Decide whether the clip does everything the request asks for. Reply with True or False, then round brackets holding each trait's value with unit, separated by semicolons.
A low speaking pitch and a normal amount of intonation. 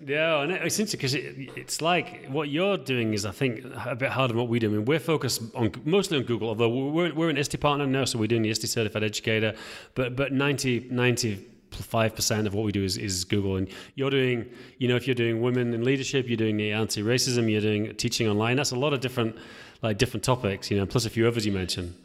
True (120 Hz; 3.7 semitones)